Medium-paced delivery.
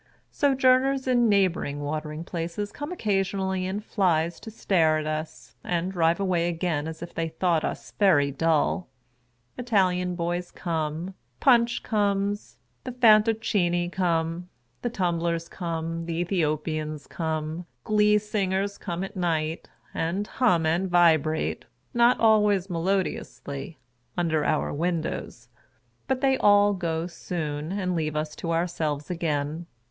No: slow, 130 wpm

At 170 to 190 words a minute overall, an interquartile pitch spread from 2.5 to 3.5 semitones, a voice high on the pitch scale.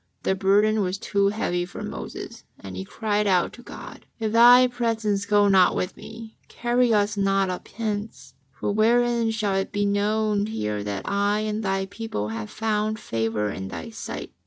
Yes: average, 180 wpm; average, 2.9 semitones; high, 205 Hz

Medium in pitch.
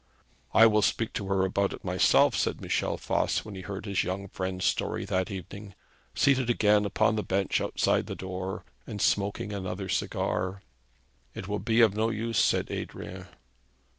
No: low, 100 Hz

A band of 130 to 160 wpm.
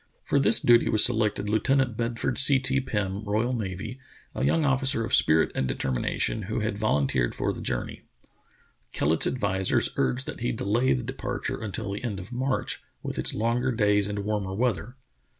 No: average, 170 wpm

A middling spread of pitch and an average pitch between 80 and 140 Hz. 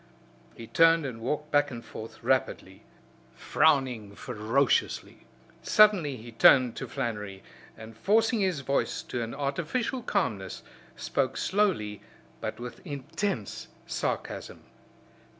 No: wide, 6.6 semitones; low, 135 Hz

